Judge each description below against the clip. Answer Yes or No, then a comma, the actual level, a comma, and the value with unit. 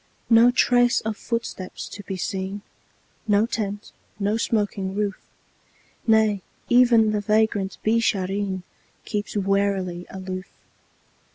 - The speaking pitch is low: No, high, 205 Hz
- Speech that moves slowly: Yes, slow, 105 wpm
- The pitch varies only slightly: Yes, narrow, 2.3 semitones